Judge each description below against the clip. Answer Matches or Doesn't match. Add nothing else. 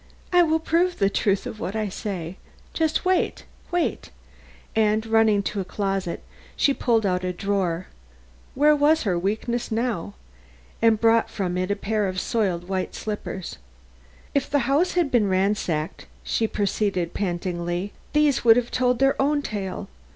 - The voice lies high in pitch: Matches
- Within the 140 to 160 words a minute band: Matches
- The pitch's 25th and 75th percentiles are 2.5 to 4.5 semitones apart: Doesn't match